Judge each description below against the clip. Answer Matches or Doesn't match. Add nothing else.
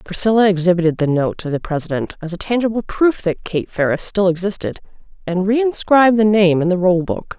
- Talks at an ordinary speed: Matches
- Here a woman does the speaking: Matches